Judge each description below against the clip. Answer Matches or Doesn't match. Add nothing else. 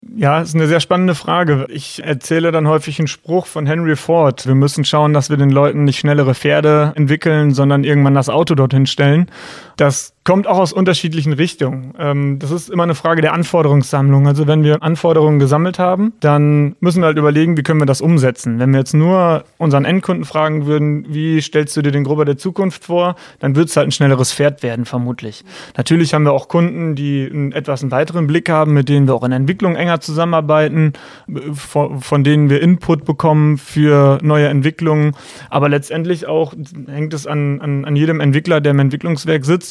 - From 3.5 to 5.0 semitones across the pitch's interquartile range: Doesn't match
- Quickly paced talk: Matches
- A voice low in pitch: Doesn't match